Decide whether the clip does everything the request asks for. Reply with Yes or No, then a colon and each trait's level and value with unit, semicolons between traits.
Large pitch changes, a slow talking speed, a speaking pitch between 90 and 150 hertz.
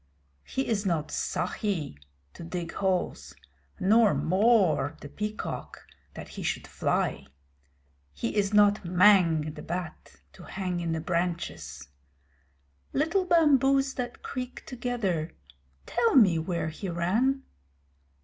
No: wide, 5.8 semitones; slow, 120 wpm; high, 190 Hz